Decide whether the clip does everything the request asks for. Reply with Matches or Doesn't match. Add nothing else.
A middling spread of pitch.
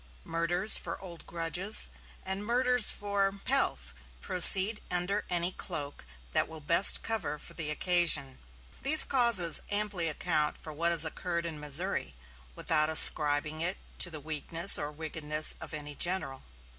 Matches